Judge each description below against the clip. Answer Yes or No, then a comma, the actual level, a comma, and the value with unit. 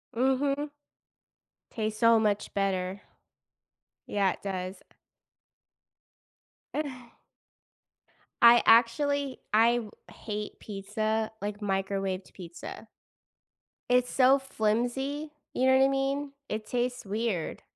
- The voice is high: Yes, high, 225 Hz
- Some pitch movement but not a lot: Yes, average, 4.4 semitones